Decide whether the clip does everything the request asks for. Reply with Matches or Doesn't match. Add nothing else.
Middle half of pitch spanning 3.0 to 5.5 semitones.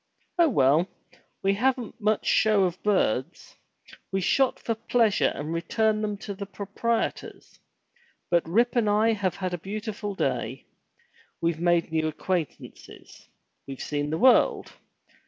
Matches